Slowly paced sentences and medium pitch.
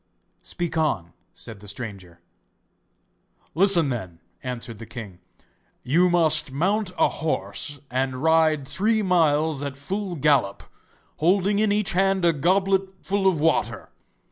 Yes: slow, 130 wpm; medium, 160 Hz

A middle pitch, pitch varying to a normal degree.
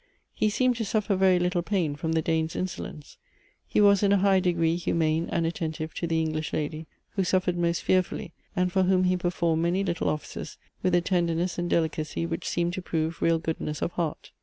No: medium, 170 Hz; narrow, 2.3 semitones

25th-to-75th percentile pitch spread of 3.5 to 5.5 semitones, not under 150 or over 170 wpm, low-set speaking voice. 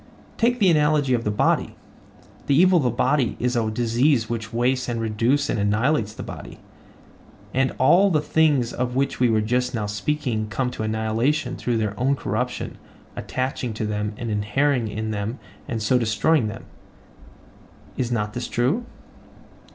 Yes: average, 4.1 semitones; average, 165 wpm; low, 120 Hz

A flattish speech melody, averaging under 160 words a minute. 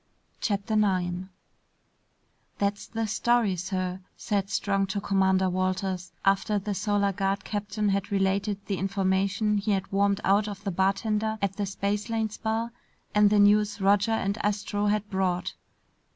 Yes: narrow, 1.5 semitones; average, 145 wpm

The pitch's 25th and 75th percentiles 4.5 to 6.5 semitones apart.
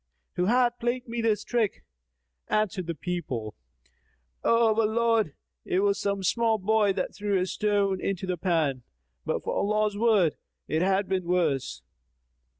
No: average, 3.6 semitones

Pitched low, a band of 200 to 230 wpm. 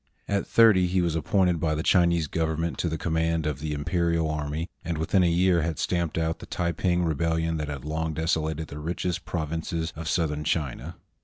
Yes: very low, 80 Hz; fast, 205 wpm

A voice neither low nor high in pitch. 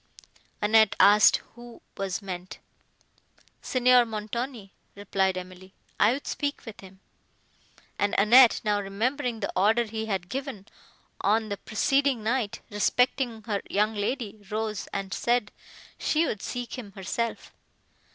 No: high, 215 Hz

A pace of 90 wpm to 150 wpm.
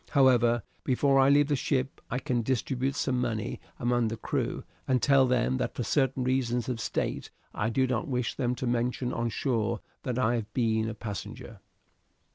No: average, 185 wpm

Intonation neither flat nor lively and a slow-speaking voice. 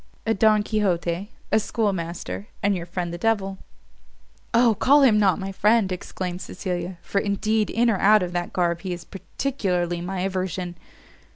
No: average, 3.4 semitones; average, 165 wpm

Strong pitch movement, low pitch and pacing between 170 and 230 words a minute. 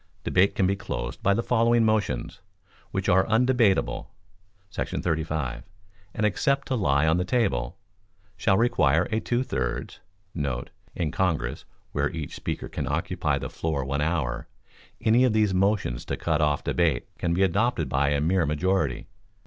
No: wide, 6.7 semitones; very low, 90 Hz; average, 155 wpm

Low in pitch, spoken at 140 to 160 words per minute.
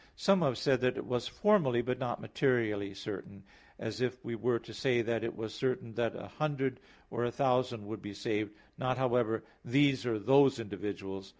No: low, 120 Hz; average, 190 wpm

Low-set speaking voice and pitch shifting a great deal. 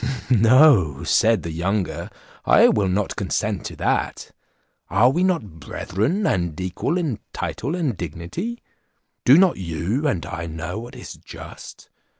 Yes: low, 105 Hz; wide, 8.8 semitones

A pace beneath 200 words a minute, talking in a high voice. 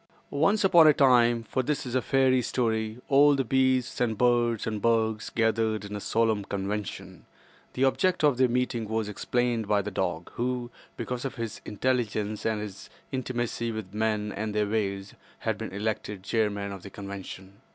No: average, 160 wpm; low, 110 Hz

